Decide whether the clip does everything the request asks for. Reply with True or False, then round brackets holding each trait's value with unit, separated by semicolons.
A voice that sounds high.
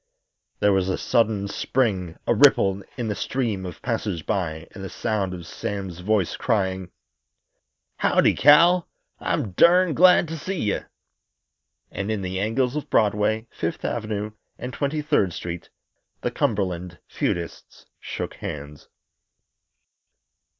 False (105 Hz)